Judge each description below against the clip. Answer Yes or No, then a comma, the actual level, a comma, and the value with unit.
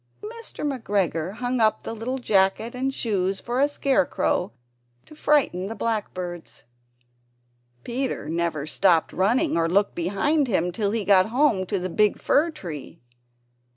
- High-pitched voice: Yes, high, 210 Hz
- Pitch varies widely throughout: Yes, wide, 6.0 semitones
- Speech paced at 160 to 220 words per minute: No, average, 150 wpm